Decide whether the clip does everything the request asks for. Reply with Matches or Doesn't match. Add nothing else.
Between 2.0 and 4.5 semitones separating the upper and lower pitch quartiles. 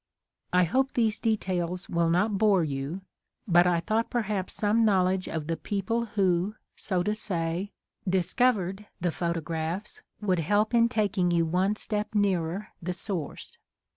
Matches